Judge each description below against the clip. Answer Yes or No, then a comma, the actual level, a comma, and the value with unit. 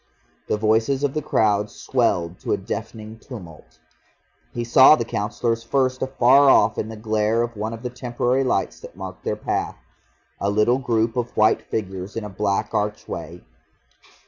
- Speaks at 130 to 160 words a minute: No, average, 170 wpm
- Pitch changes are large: No, average, 2.8 semitones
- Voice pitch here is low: Yes, low, 110 Hz